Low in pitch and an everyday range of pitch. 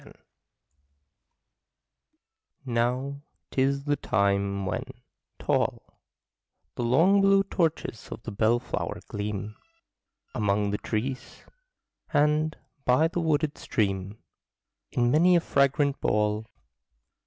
No: low, 125 Hz; wide, 6.0 semitones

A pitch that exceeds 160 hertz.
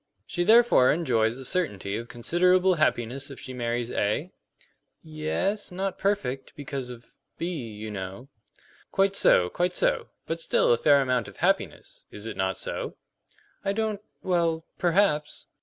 No: medium, 150 Hz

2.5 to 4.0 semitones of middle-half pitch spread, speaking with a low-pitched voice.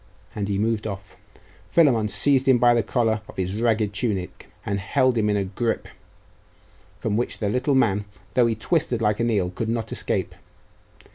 Yes: average, 2.8 semitones; low, 110 Hz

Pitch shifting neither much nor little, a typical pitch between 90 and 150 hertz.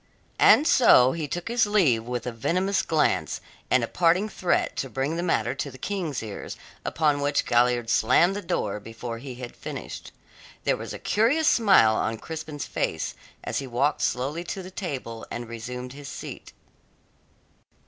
No: wide, 6.5 semitones; medium, 140 Hz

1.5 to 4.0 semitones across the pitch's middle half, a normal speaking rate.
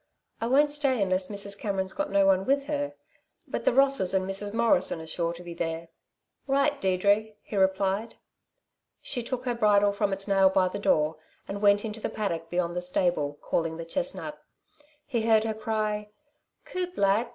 Yes: average, 3.7 semitones; average, 185 wpm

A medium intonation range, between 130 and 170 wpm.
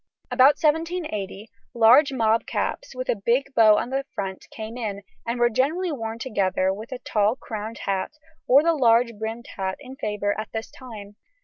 No: average, 3.9 semitones; average, 180 wpm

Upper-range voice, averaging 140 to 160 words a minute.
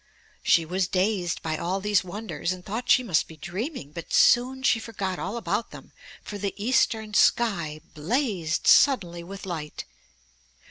Yes: high, 195 Hz; average, 155 wpm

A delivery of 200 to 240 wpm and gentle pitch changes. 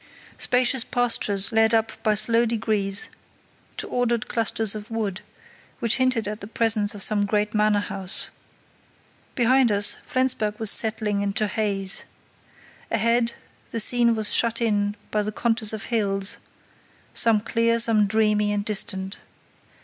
No: average, 140 wpm; narrow, 2.0 semitones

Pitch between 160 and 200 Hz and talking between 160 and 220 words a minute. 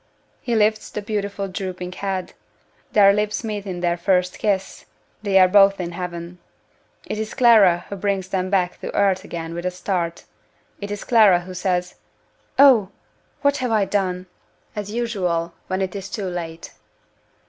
Yes: high, 190 Hz; average, 165 wpm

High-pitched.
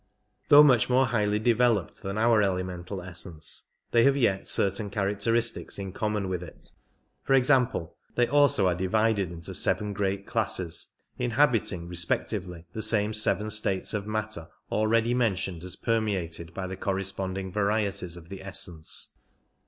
No: low, 100 Hz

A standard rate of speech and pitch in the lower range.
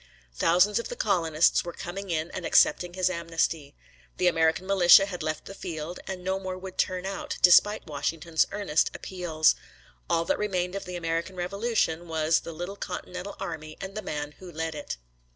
No: average, 180 wpm; medium, 175 Hz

